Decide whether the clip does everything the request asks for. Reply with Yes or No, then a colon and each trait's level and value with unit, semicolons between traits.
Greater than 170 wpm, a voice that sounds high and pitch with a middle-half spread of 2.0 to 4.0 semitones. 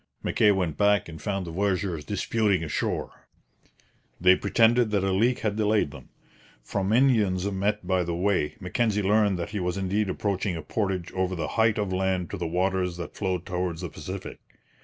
No: average, 180 wpm; very low, 95 Hz; narrow, 2.4 semitones